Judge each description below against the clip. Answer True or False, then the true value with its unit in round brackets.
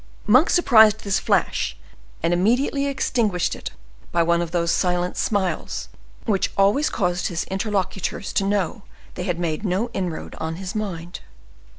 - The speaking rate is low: False (150 wpm)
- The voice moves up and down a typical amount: True (3.6 semitones)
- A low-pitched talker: False (190 Hz)